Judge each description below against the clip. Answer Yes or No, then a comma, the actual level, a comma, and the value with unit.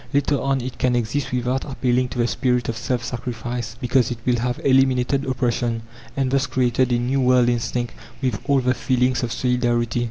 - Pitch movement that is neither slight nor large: No, narrow, 1.3 semitones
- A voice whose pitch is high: No, low, 125 Hz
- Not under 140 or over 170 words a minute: No, average, 190 wpm